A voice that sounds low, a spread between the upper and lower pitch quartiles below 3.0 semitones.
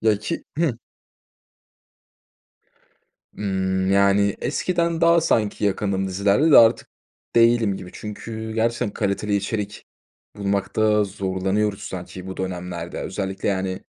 Yes: low, 100 Hz; narrow, 2.6 semitones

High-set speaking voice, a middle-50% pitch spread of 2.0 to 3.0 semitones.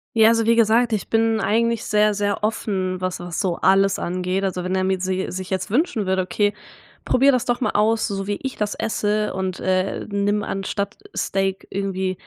Yes: high, 200 Hz; average, 2.7 semitones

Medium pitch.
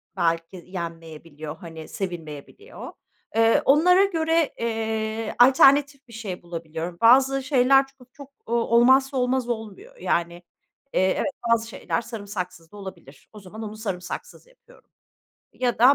No: high, 225 Hz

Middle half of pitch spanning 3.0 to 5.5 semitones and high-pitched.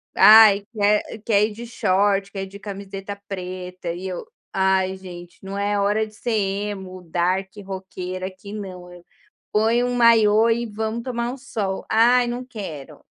No: narrow, 2.6 semitones; high, 200 Hz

